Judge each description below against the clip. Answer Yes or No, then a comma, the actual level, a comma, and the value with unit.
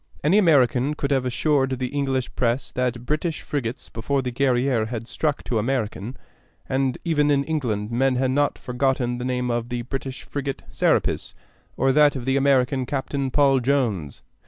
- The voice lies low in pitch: Yes, low, 130 Hz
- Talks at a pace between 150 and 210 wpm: Yes, average, 170 wpm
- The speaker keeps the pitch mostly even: Yes, narrow, 2.3 semitones